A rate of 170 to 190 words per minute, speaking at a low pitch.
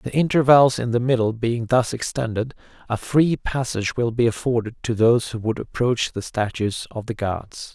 Yes: average, 185 wpm; low, 120 Hz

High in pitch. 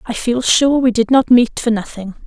Yes: high, 235 Hz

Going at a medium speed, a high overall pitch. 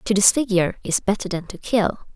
Yes: average, 195 wpm; high, 200 Hz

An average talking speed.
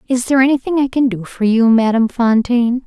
No: fast, 210 wpm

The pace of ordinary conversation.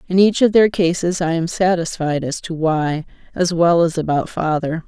Yes: average, 195 wpm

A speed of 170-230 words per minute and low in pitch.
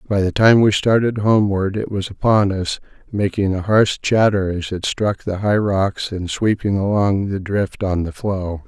Yes: average, 195 wpm; low, 100 Hz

